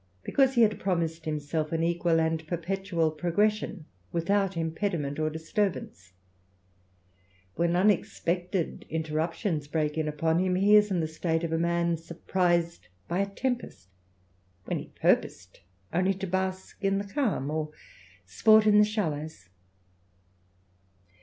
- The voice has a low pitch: No, medium, 170 Hz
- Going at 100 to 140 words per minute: Yes, slow, 135 wpm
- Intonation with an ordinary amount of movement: Yes, average, 3.5 semitones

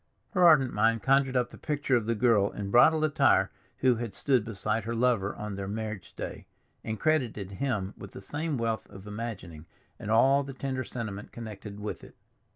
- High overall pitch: No, low, 115 Hz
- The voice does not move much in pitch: No, average, 4.3 semitones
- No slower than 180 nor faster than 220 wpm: Yes, average, 190 wpm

